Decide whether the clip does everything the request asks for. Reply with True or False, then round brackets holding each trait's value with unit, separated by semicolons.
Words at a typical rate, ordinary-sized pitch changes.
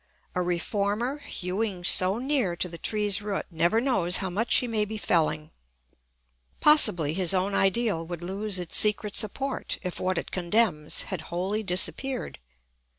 True (150 wpm; 3.7 semitones)